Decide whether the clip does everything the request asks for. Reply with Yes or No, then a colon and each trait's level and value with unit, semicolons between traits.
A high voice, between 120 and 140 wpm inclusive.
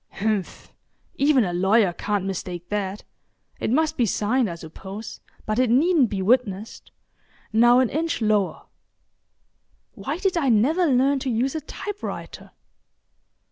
Yes: high, 230 Hz; slow, 135 wpm